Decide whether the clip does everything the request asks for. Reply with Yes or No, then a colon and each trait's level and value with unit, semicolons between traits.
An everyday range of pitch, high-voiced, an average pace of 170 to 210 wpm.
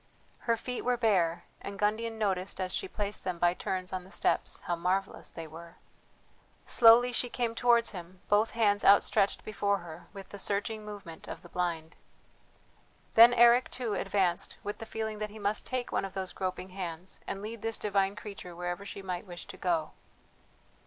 Yes: average, 3.5 semitones; high, 200 Hz; average, 185 wpm